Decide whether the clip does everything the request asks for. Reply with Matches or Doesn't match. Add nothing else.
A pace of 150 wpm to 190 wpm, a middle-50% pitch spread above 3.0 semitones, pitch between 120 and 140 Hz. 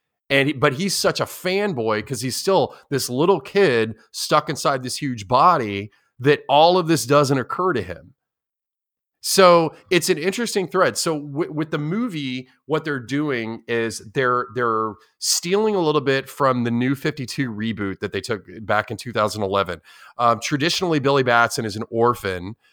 Matches